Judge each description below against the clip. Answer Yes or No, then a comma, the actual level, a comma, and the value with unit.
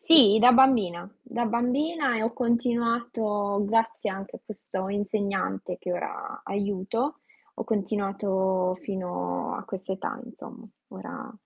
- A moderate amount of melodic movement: Yes, average, 3.9 semitones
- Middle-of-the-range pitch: No, high, 215 Hz